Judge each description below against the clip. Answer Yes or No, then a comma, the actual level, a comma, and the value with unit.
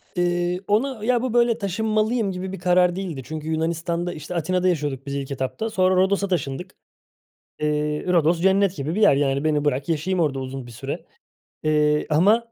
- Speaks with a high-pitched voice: No, medium, 175 Hz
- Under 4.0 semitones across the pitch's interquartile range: No, average, 4.3 semitones